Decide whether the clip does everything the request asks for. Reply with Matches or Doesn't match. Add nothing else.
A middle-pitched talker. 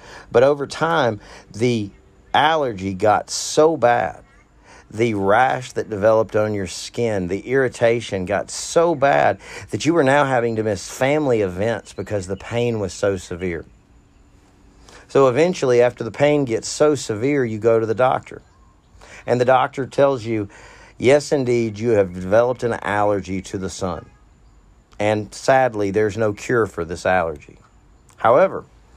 Doesn't match